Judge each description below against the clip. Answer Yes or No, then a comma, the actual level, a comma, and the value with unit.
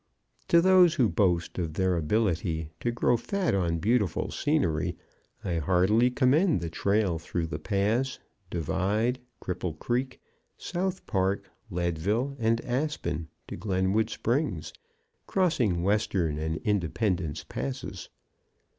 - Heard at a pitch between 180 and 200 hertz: No, low, 100 Hz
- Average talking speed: No, slow, 120 wpm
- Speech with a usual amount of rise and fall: No, wide, 6.4 semitones